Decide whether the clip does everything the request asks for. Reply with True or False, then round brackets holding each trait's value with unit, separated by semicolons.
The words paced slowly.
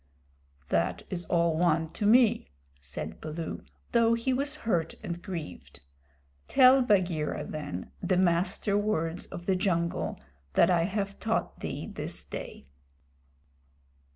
True (125 wpm)